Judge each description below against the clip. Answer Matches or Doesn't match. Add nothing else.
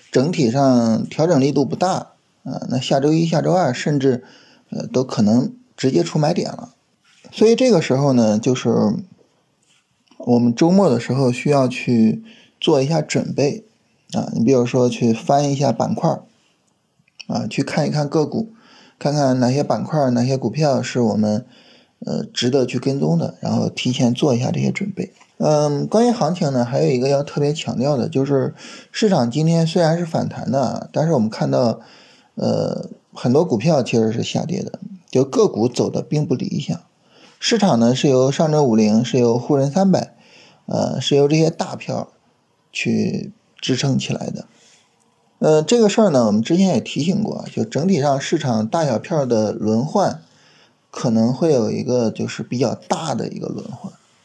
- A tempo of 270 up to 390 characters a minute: Doesn't match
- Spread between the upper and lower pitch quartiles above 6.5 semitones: Doesn't match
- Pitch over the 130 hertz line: Matches